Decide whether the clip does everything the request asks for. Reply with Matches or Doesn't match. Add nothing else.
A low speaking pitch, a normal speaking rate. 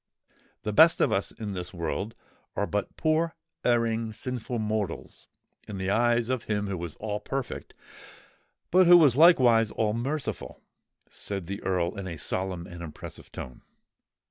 Matches